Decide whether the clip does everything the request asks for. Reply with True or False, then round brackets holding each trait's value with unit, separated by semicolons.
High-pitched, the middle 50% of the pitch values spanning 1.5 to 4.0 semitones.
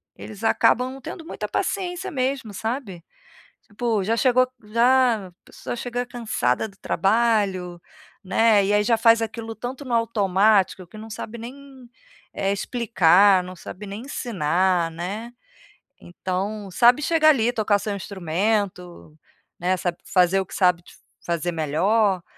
False (210 Hz; 4.4 semitones)